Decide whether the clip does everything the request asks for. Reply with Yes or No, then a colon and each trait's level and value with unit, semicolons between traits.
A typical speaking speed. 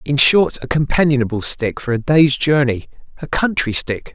Yes: average, 175 wpm